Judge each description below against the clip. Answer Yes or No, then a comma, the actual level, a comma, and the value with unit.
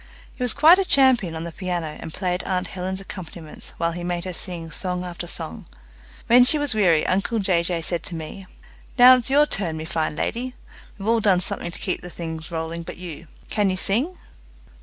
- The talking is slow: No, fast, 205 wpm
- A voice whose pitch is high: No, medium, 180 Hz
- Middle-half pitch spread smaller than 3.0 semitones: No, average, 4.8 semitones